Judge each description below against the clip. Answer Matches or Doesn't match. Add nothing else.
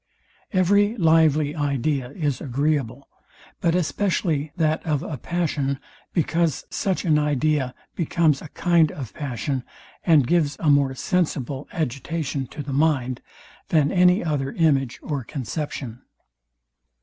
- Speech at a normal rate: Doesn't match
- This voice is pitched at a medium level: Matches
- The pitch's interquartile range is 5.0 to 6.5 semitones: Doesn't match